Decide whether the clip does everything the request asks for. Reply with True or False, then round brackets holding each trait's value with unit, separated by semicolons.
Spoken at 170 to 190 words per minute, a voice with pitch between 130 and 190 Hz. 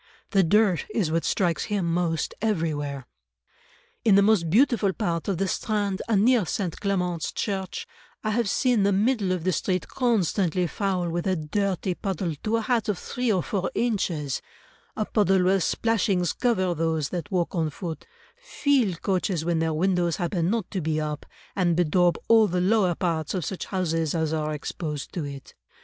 True (180 wpm; 185 Hz)